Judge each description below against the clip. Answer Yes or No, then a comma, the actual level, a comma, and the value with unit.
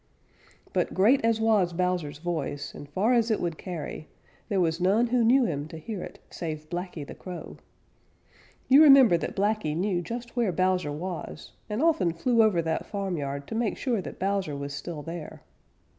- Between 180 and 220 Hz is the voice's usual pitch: Yes, medium, 185 Hz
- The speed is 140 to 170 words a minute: No, average, 180 wpm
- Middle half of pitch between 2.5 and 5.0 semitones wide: No, wide, 5.6 semitones